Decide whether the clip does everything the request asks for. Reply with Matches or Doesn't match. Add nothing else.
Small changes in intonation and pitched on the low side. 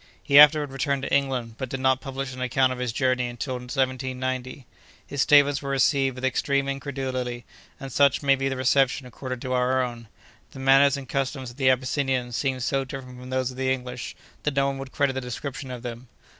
Matches